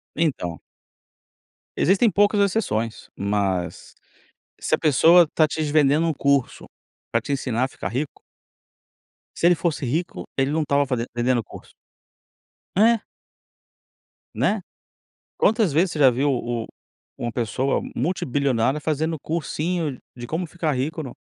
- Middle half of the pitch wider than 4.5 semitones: Yes, average, 4.9 semitones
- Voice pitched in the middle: Yes, medium, 145 Hz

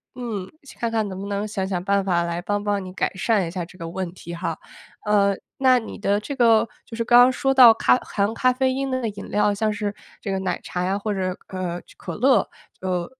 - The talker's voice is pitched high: Yes, high, 205 Hz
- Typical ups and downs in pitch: Yes, average, 3.7 semitones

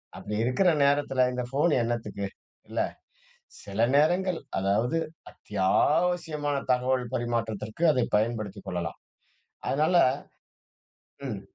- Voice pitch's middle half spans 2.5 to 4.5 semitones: No, wide, 5.6 semitones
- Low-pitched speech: Yes, low, 125 Hz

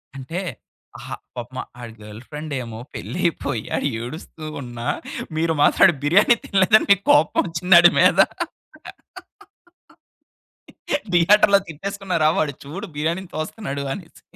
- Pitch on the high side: No, medium, 160 Hz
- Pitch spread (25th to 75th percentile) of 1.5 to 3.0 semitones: No, average, 5.1 semitones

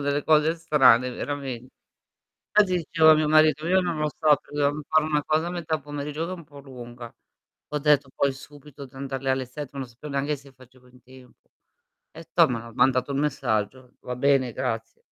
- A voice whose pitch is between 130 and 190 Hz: Yes, medium, 140 Hz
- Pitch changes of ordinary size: Yes, average, 3.0 semitones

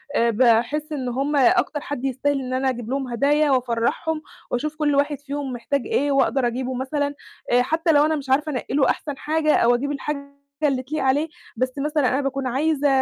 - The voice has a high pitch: Yes, very high, 275 Hz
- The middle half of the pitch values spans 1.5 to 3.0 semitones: Yes, narrow, 2.5 semitones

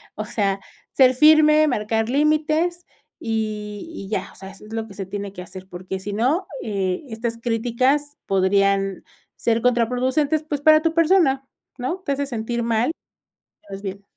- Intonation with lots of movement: Yes, wide, 6.3 semitones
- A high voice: Yes, high, 230 Hz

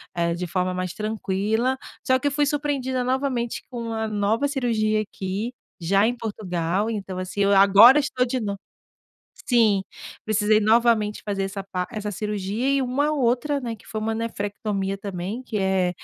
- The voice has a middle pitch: No, high, 215 Hz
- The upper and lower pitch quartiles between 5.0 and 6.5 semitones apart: No, average, 3.9 semitones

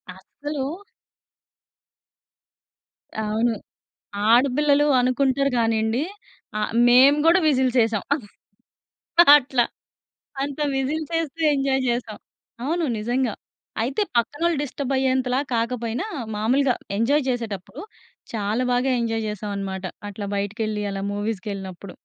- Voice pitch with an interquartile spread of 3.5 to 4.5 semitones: Yes, average, 4.2 semitones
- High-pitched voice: Yes, high, 245 Hz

